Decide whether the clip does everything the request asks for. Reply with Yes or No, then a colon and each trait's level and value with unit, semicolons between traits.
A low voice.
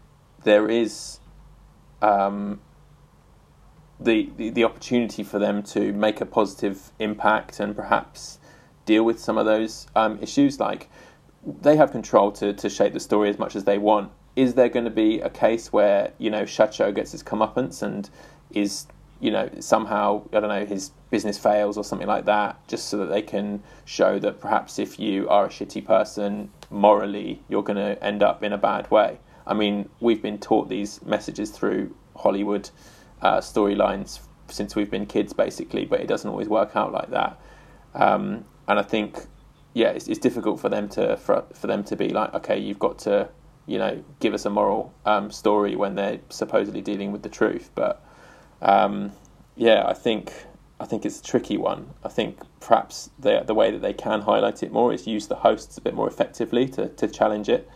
Yes: low, 105 Hz